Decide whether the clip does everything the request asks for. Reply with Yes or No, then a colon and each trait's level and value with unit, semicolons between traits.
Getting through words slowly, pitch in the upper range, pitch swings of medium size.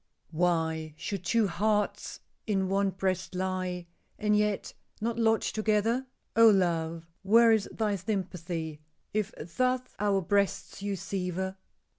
Yes: slow, 125 wpm; high, 195 Hz; average, 3.0 semitones